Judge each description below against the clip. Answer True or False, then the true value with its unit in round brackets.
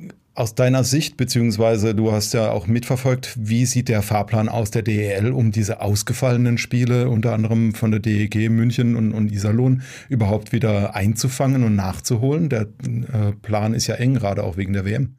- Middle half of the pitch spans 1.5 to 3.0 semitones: True (2.5 semitones)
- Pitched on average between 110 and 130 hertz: True (115 Hz)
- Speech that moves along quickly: False (180 wpm)